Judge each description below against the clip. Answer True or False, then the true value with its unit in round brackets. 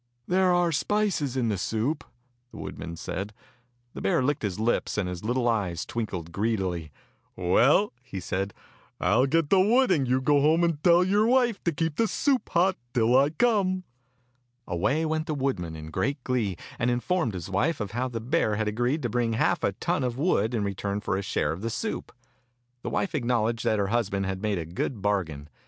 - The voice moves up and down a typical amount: False (7.9 semitones)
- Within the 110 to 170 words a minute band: False (205 wpm)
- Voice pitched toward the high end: False (120 Hz)